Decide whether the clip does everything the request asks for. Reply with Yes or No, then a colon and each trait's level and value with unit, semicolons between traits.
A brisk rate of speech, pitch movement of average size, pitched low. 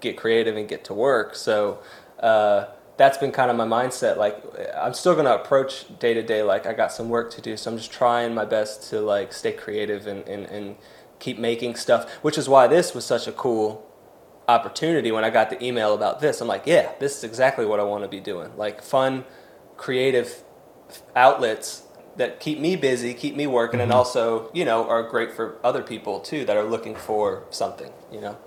Yes: fast, 215 wpm; average, 4.0 semitones; low, 120 Hz